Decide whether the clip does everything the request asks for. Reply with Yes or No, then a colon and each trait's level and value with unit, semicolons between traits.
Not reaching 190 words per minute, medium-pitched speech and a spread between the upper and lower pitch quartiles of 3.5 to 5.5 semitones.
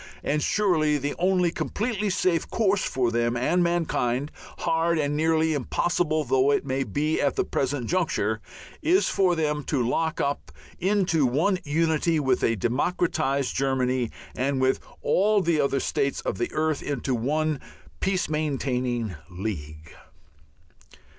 Yes: average, 140 wpm; medium, 150 Hz; average, 4.7 semitones